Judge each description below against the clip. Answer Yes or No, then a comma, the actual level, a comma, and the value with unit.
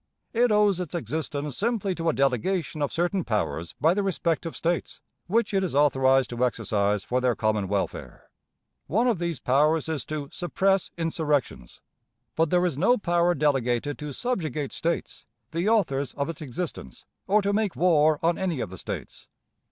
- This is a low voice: No, medium, 160 Hz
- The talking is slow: No, average, 170 wpm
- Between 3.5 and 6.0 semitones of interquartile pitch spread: Yes, average, 5.2 semitones